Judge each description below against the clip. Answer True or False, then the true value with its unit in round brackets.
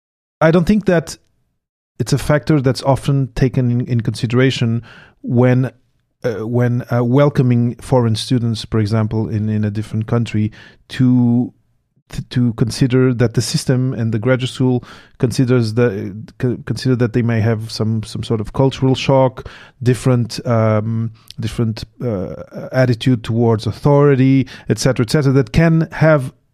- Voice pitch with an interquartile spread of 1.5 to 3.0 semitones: True (2.7 semitones)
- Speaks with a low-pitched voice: True (125 Hz)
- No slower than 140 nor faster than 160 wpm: True (145 wpm)